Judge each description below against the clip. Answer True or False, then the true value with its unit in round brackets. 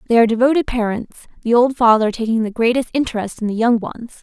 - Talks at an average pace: False (215 wpm)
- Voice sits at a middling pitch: False (230 Hz)